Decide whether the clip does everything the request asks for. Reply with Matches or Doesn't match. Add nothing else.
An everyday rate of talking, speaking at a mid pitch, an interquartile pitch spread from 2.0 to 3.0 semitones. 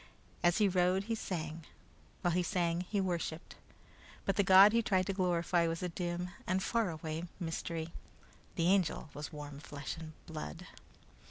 Matches